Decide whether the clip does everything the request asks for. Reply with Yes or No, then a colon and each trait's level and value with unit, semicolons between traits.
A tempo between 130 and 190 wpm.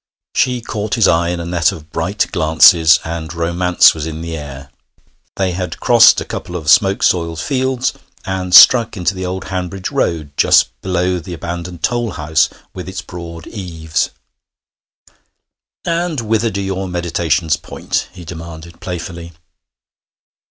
Yes: average, 150 wpm